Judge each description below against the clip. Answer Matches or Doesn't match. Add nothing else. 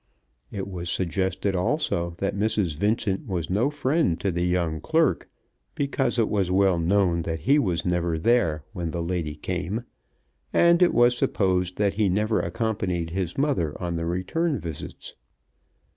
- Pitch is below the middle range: Matches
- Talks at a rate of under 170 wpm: Matches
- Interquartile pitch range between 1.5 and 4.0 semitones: Doesn't match